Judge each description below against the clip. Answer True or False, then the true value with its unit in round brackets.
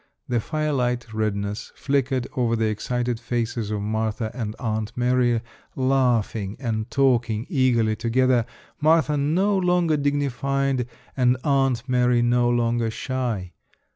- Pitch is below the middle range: True (125 Hz)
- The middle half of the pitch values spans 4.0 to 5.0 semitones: False (3.2 semitones)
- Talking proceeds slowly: True (120 wpm)